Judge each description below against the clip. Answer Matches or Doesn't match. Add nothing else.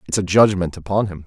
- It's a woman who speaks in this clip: Doesn't match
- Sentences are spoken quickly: Matches